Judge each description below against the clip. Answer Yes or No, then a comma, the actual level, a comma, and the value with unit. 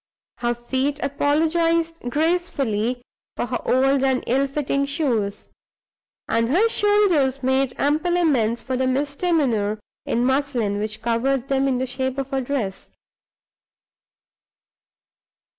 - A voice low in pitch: No, very high, 270 Hz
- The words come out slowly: Yes, slow, 120 wpm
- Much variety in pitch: No, average, 3.2 semitones